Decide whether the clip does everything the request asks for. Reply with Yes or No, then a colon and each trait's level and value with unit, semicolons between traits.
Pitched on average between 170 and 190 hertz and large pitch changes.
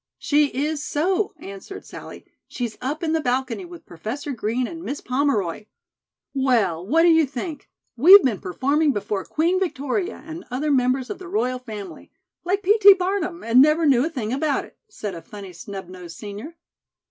No: very high, 275 Hz; wide, 6.3 semitones